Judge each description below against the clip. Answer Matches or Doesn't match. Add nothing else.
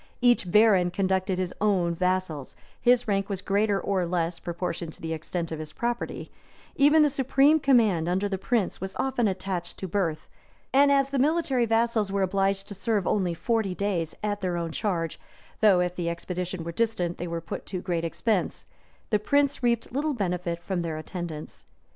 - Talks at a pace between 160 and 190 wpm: Matches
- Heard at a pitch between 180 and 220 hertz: Matches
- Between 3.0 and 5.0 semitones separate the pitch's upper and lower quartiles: Matches